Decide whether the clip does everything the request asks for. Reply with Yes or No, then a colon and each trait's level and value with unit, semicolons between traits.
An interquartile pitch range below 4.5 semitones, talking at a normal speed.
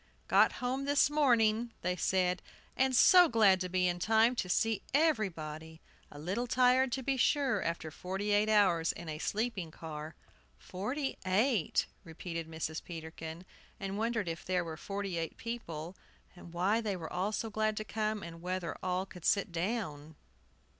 No: average, 5.1 semitones; average, 165 wpm